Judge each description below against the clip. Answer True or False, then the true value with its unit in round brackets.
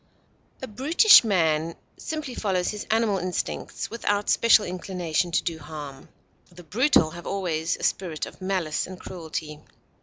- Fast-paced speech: False (145 wpm)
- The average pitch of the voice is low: False (185 Hz)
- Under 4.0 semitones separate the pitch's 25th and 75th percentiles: False (4.4 semitones)